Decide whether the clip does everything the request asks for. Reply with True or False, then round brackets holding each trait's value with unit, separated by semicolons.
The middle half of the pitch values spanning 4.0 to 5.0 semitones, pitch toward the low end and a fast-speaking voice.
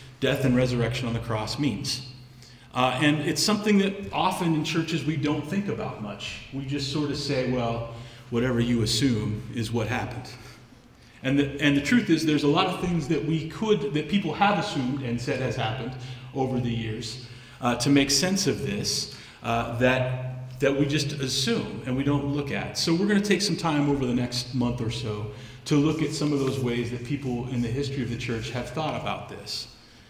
False (3.5 semitones; 130 Hz; 210 wpm)